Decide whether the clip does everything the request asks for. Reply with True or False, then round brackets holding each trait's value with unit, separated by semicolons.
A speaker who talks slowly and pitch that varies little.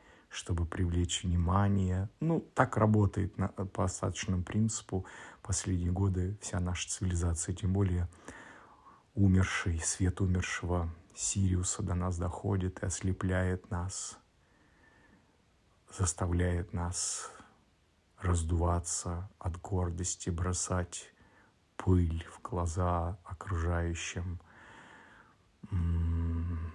True (80 wpm; 2.0 semitones)